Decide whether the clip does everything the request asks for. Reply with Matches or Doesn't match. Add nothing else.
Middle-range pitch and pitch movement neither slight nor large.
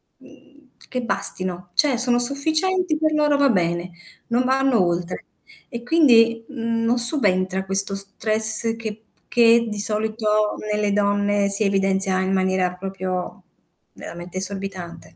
Doesn't match